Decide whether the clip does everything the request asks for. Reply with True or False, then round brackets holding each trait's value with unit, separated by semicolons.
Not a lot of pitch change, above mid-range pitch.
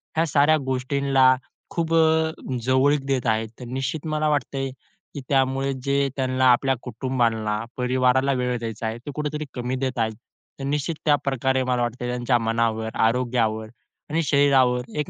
False (2.3 semitones; 130 Hz)